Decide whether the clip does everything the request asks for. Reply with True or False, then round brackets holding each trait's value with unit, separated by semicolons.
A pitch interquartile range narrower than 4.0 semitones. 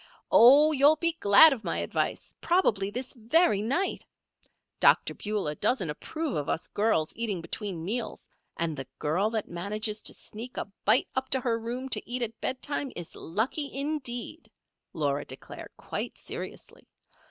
False (5.2 semitones)